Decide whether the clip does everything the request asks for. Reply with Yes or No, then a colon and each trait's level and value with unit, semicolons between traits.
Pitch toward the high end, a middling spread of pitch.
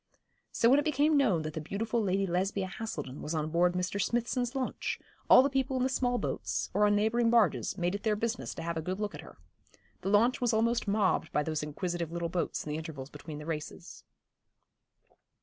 No: high, 195 Hz; wide, 6.2 semitones